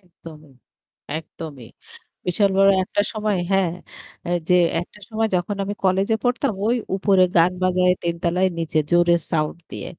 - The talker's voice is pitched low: No, medium, 180 Hz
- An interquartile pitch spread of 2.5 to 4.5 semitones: Yes, average, 2.8 semitones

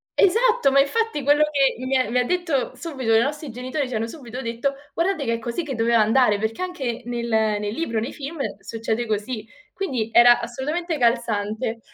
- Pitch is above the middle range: Yes, very high, 250 Hz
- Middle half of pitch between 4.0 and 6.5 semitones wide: Yes, average, 4.6 semitones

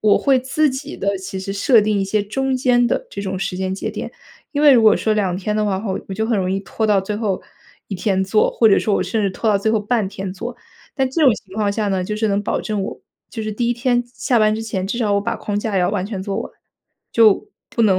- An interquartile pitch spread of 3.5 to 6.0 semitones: No, average, 2.8 semitones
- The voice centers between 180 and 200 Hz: No, high, 210 Hz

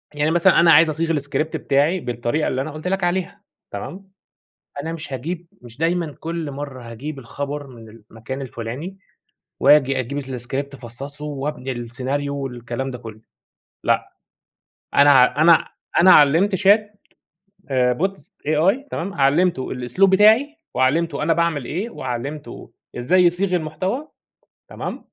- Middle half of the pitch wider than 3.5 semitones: Yes, average, 4.6 semitones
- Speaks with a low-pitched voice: No, medium, 145 Hz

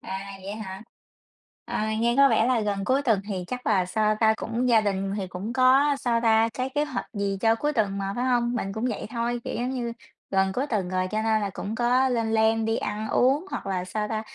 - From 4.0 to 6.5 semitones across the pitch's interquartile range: No, average, 3.6 semitones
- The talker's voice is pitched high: Yes, high, 220 Hz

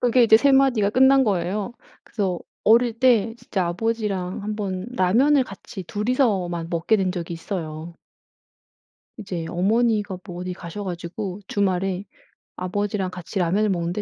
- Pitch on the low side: No, high, 195 Hz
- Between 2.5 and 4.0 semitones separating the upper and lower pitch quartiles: Yes, average, 3.7 semitones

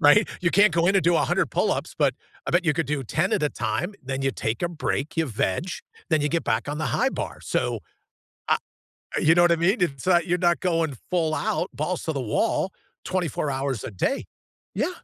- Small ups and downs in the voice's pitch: No, average, 4.1 semitones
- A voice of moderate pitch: Yes, medium, 160 Hz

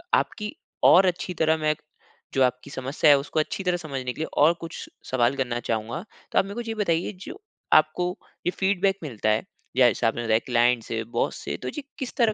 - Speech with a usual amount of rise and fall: No, wide, 6.7 semitones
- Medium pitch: Yes, medium, 150 Hz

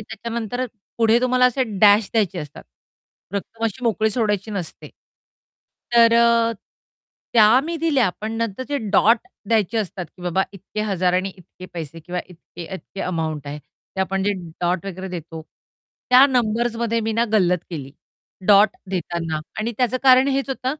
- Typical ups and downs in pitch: Yes, average, 4.5 semitones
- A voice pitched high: Yes, high, 215 Hz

